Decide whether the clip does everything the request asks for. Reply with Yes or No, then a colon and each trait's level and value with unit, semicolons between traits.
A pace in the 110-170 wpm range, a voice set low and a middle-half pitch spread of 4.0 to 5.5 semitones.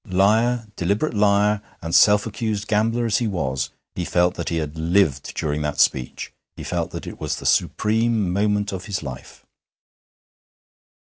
Yes: average, 165 wpm; low, 100 Hz; average, 4.5 semitones